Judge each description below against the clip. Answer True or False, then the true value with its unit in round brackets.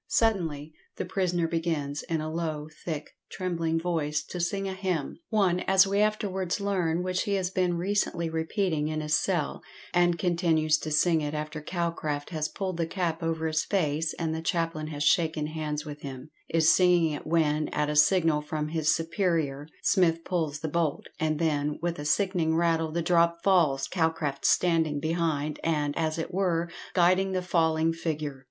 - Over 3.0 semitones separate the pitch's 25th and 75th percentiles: False (2.5 semitones)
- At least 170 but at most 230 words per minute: True (175 wpm)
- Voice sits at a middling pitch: True (165 Hz)